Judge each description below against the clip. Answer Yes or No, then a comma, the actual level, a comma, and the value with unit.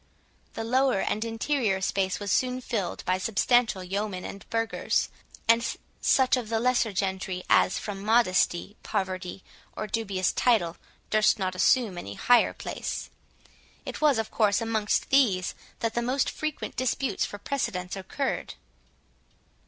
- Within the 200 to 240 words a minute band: No, average, 140 wpm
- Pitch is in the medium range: No, high, 215 Hz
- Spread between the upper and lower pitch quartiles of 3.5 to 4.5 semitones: Yes, average, 4.2 semitones